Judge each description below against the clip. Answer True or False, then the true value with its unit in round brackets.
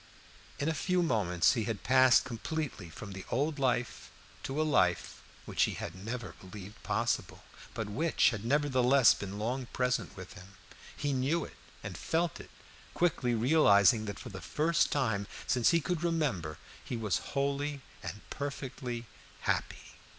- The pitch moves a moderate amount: False (5.7 semitones)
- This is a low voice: True (125 Hz)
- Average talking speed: True (160 wpm)